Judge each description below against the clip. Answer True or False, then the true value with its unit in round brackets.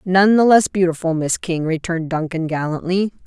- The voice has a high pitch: False (175 Hz)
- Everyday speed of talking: True (165 wpm)